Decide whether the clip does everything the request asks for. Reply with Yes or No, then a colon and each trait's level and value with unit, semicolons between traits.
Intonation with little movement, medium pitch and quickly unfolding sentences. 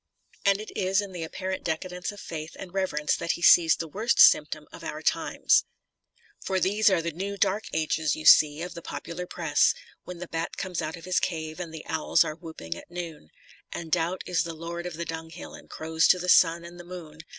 Yes: narrow, 2.2 semitones; medium, 170 Hz; fast, 220 wpm